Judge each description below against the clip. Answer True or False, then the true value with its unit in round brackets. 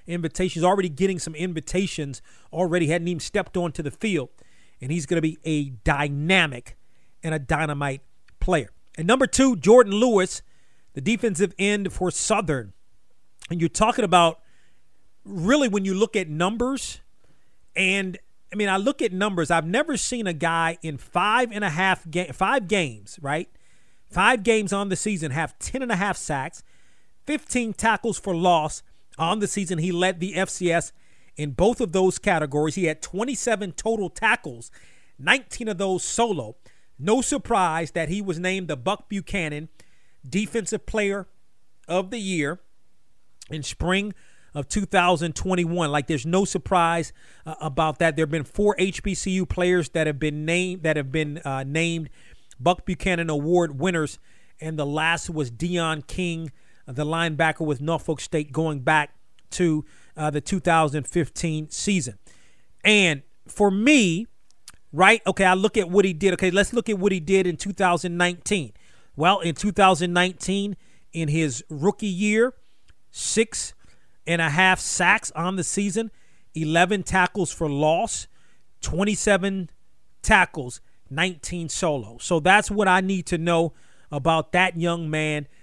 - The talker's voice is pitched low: False (175 Hz)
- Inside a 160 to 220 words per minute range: False (150 wpm)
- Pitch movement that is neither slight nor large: True (4.0 semitones)